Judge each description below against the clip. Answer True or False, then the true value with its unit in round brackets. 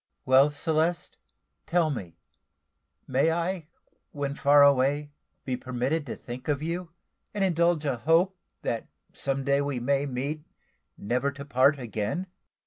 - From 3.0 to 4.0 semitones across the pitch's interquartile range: True (3.7 semitones)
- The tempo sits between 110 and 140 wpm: True (135 wpm)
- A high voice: False (140 Hz)